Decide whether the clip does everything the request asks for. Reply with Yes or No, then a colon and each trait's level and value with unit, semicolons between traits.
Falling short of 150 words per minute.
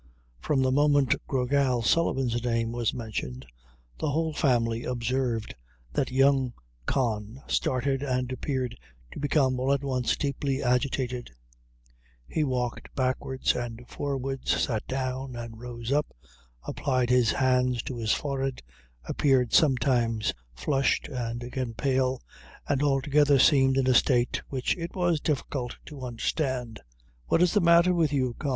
Yes: average, 140 wpm